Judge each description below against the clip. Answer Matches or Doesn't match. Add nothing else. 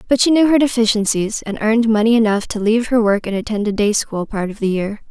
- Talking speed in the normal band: Doesn't match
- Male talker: Doesn't match